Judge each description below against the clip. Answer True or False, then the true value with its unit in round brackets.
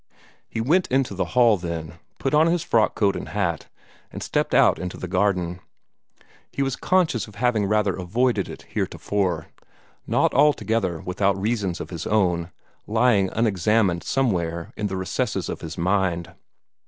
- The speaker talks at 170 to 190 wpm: False (155 wpm)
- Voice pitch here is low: True (100 Hz)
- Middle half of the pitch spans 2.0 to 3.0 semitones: False (4.6 semitones)